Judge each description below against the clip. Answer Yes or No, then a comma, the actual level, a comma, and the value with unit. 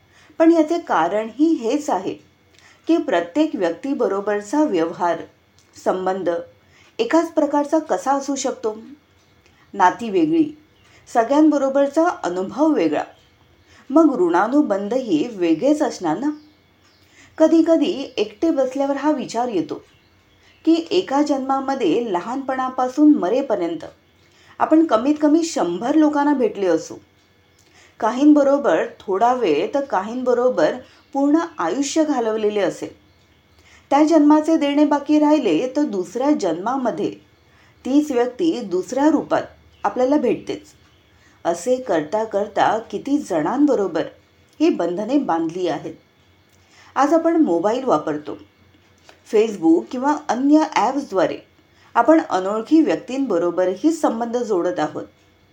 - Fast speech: No, average, 95 wpm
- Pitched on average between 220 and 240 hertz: No, very high, 275 Hz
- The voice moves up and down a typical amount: No, wide, 7.1 semitones